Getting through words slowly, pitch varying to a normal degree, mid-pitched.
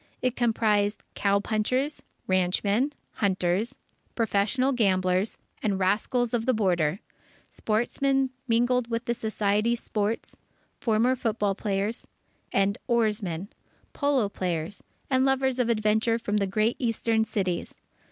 No: slow, 115 wpm; average, 3.2 semitones; high, 220 Hz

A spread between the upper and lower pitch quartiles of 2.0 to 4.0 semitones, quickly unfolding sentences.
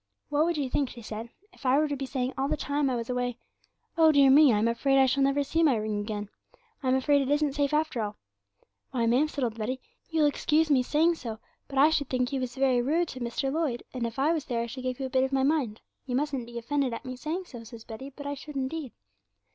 Yes: average, 3.2 semitones; fast, 265 wpm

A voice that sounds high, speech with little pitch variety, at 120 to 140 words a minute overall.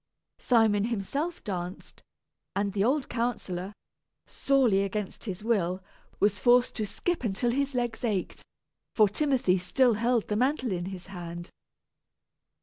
No: high, 215 Hz; average, 4.2 semitones; slow, 135 wpm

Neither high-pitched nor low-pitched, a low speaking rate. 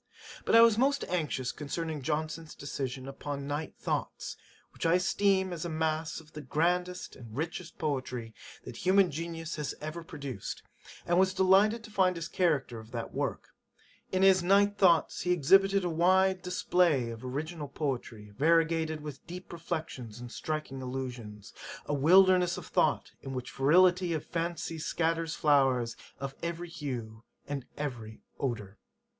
No: medium, 160 Hz; average, 165 wpm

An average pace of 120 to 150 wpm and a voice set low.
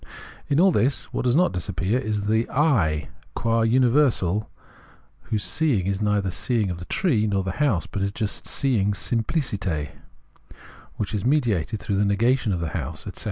No: average, 175 wpm; low, 105 Hz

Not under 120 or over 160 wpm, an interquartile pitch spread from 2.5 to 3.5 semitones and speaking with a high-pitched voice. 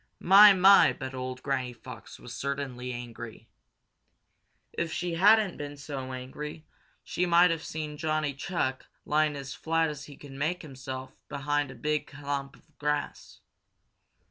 No: average, 145 wpm; average, 3.2 semitones; medium, 145 Hz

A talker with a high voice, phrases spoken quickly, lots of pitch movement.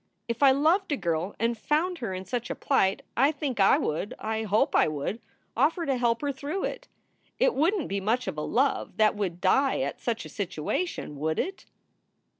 Yes: high, 235 Hz; fast, 210 wpm; wide, 6.7 semitones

